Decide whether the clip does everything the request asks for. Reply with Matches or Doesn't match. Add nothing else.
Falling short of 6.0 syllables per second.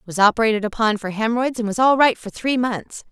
Doesn't match